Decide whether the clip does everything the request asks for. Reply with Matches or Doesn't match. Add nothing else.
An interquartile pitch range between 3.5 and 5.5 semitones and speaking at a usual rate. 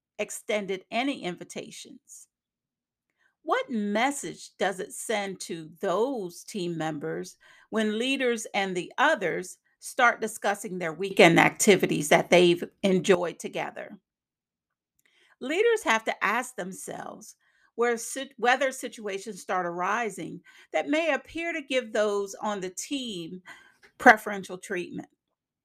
Doesn't match